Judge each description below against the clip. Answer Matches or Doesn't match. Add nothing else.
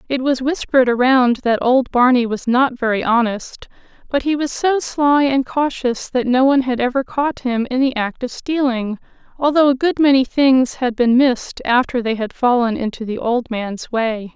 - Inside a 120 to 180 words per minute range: Doesn't match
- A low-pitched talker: Doesn't match